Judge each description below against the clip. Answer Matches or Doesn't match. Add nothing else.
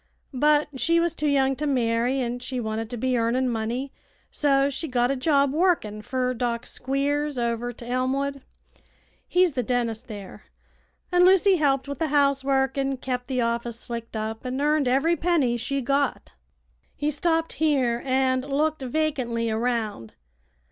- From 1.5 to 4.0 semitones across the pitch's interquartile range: Matches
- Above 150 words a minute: Matches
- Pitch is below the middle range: Doesn't match